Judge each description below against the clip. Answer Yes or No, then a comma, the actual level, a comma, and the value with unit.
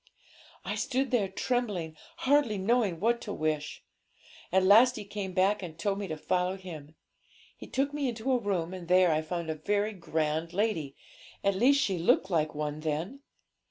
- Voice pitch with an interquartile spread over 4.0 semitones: Yes, average, 5.3 semitones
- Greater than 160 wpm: Yes, average, 180 wpm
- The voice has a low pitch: No, high, 190 Hz